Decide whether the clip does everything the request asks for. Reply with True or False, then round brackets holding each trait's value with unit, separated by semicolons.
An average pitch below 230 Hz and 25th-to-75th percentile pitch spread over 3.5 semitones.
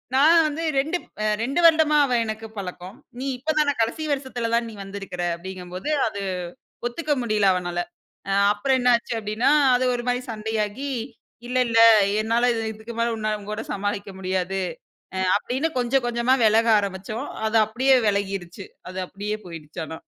True (220 Hz; 4.2 semitones)